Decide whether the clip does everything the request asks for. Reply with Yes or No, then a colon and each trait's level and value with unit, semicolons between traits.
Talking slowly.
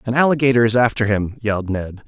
No: fast, 205 wpm